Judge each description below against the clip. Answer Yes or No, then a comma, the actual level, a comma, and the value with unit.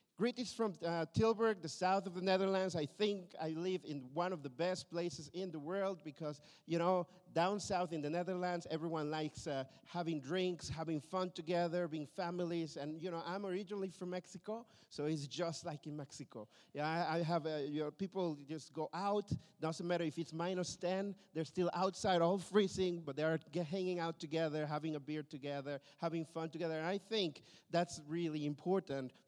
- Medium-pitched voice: Yes, medium, 170 Hz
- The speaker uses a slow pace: No, average, 195 wpm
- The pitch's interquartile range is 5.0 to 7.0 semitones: No, average, 3.0 semitones